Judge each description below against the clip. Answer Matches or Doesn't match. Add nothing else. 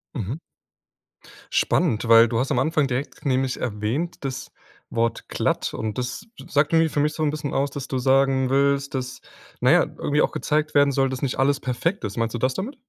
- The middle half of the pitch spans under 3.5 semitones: Matches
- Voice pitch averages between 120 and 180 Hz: Matches